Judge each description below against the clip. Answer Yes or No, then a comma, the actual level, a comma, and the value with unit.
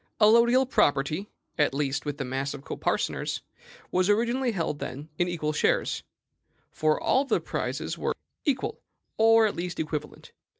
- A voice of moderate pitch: Yes, medium, 175 Hz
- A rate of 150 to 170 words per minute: Yes, average, 155 wpm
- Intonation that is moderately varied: No, wide, 7.5 semitones